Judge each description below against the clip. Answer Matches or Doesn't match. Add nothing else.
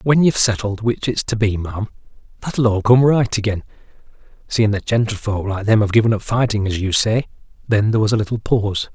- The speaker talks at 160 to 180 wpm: Doesn't match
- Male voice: Matches